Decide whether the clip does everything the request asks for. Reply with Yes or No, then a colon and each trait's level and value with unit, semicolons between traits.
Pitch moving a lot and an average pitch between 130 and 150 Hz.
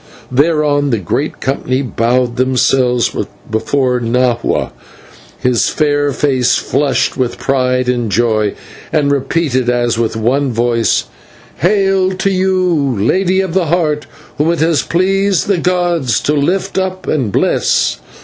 Yes: wide, 5.7 semitones; medium, 140 Hz